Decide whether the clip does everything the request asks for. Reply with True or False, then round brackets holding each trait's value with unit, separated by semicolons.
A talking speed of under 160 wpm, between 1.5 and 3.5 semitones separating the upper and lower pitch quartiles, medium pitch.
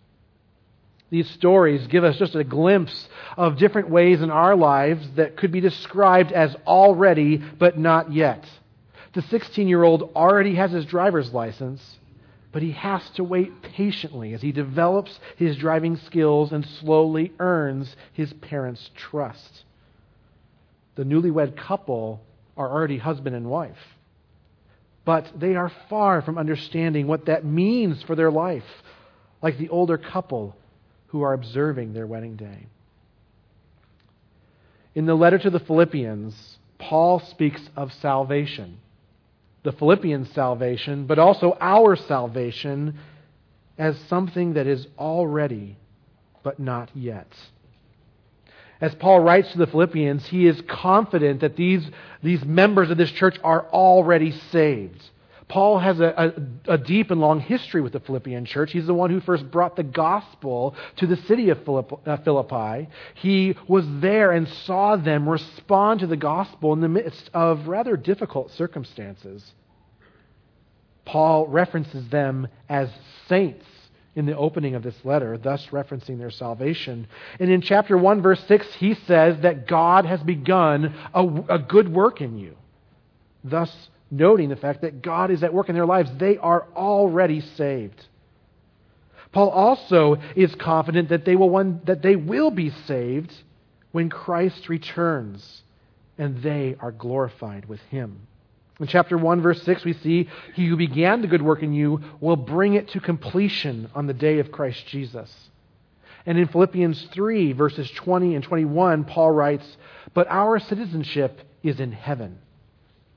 False (150 wpm; 4.9 semitones; 155 Hz)